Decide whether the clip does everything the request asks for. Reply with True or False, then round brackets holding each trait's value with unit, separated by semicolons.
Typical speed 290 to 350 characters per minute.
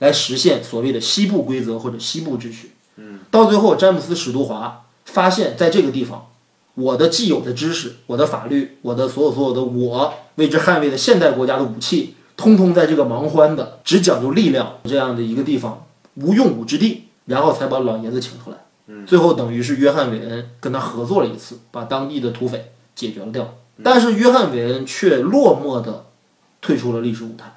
True (310 characters per minute)